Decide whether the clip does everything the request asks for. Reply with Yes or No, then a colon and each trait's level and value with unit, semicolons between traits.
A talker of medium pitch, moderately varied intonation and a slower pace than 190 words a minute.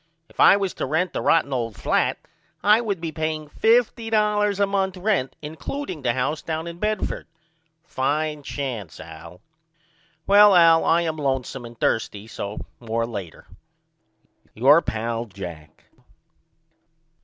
No: medium, 155 Hz; wide, 8.5 semitones; slow, 135 wpm